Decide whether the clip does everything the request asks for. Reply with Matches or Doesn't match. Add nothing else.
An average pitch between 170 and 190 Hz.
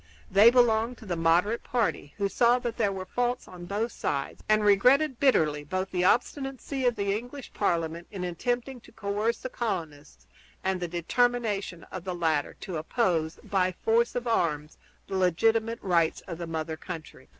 Doesn't match